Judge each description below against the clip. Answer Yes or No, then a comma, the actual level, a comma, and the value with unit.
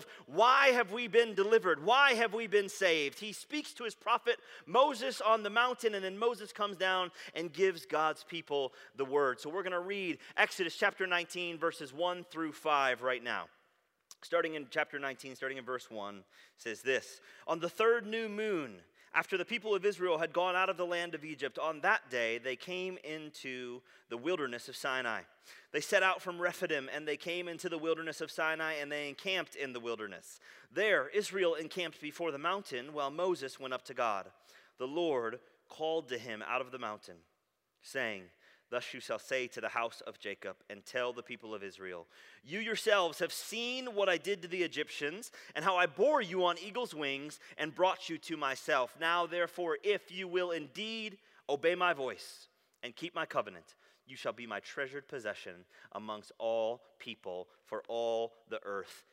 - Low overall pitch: No, medium, 170 Hz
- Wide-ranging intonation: Yes, wide, 6.0 semitones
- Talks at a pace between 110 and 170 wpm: No, average, 190 wpm